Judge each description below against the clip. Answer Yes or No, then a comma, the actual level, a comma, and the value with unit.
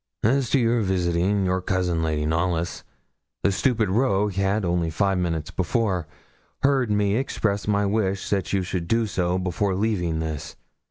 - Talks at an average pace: Yes, average, 160 wpm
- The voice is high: No, very low, 95 Hz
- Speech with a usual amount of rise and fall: Yes, average, 3.1 semitones